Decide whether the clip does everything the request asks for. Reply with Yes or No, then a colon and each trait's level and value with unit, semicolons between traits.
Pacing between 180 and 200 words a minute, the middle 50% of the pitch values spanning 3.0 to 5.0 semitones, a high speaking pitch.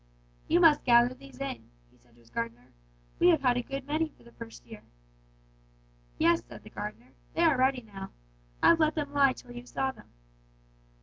Yes: average, 190 wpm; average, 4.2 semitones; very high, 255 Hz